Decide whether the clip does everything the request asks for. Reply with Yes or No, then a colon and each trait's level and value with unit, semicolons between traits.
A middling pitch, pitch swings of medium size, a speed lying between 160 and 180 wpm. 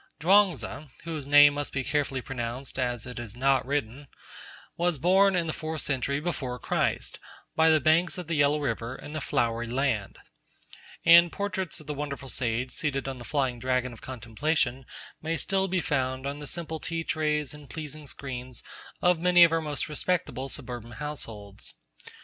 Yes: medium, 145 Hz; average, 3.9 semitones; average, 175 wpm